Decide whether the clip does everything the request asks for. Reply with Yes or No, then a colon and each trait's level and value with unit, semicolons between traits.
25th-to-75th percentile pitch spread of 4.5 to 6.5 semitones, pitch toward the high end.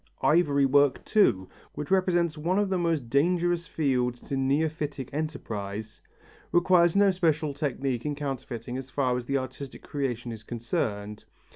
No: average, 5.0 semitones; medium, 140 Hz